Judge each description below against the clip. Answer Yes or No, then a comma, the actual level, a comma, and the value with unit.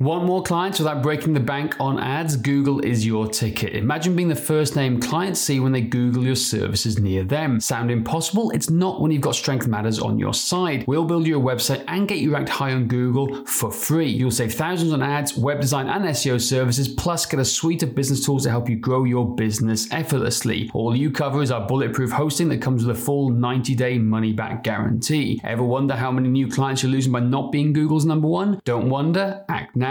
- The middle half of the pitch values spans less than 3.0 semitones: No, average, 4.0 semitones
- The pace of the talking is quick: Yes, fast, 225 wpm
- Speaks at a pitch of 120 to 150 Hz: Yes, low, 135 Hz